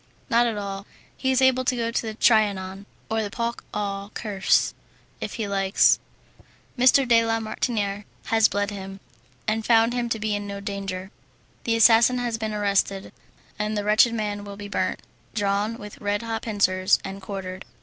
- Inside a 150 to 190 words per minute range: Yes, average, 180 wpm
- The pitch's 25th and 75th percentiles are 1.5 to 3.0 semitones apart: Yes, narrow, 2.4 semitones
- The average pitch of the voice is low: No, high, 210 Hz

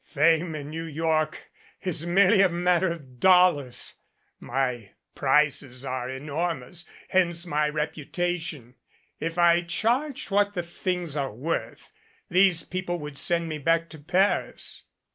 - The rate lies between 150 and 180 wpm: No, average, 140 wpm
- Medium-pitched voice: Yes, medium, 165 Hz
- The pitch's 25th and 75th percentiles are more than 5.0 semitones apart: No, average, 3.3 semitones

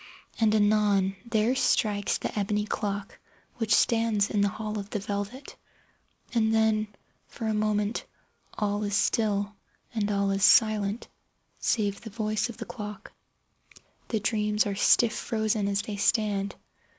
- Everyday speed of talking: Yes, average, 145 wpm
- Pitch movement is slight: Yes, narrow, 1.3 semitones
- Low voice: No, high, 210 Hz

